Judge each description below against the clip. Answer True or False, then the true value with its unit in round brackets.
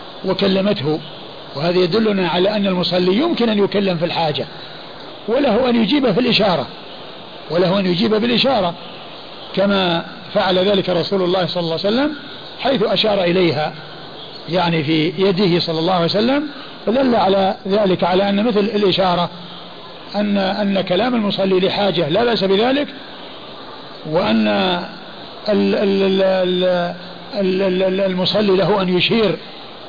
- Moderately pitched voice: False (195 Hz)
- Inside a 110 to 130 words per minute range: True (120 wpm)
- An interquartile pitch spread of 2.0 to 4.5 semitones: True (2.6 semitones)